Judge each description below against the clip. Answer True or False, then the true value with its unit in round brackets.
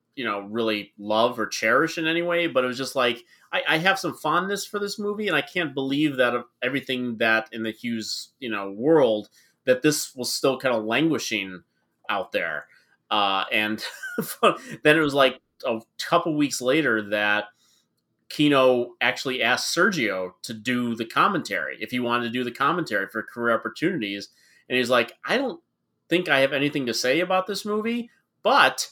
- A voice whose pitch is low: True (125 Hz)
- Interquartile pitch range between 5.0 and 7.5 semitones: True (5.4 semitones)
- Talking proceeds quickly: False (185 wpm)